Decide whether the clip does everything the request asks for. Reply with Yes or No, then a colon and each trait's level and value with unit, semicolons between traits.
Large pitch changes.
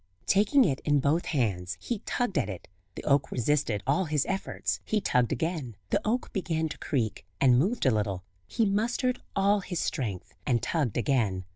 Yes: wide, 8.6 semitones